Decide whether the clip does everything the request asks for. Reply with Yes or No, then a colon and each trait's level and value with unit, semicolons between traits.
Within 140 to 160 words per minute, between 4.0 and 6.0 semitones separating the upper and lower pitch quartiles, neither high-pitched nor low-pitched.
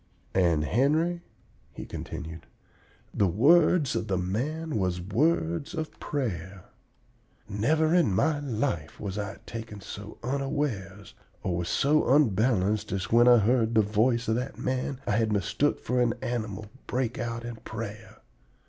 No: average, 145 wpm; wide, 5.6 semitones; low, 115 Hz